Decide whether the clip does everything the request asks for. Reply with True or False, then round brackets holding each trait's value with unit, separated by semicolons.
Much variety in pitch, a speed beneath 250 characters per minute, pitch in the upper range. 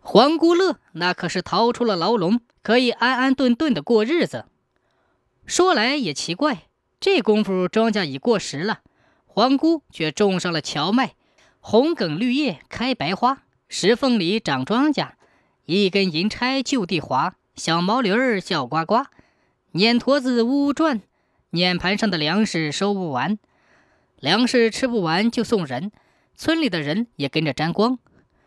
True (6.0 semitones; 215 characters per minute; 220 Hz)